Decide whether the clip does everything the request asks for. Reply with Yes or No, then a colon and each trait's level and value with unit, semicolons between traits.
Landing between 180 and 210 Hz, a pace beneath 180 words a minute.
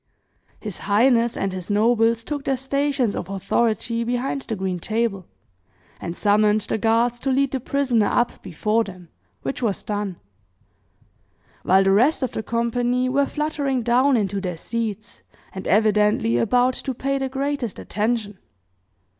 No: high, 230 Hz; average, 150 wpm